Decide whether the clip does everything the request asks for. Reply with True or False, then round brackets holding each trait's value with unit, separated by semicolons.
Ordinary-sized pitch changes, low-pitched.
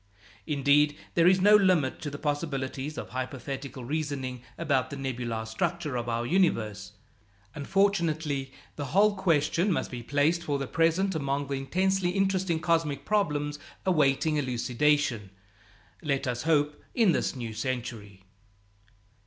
False (4.4 semitones; 145 Hz)